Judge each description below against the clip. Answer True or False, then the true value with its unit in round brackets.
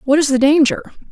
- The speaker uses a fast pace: True (215 wpm)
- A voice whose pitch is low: False (290 Hz)